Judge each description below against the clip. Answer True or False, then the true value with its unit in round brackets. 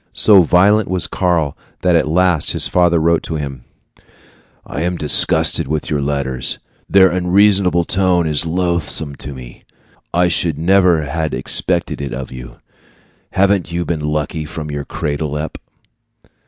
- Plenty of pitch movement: False (3.4 semitones)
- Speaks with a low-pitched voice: True (80 Hz)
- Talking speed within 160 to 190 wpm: False (150 wpm)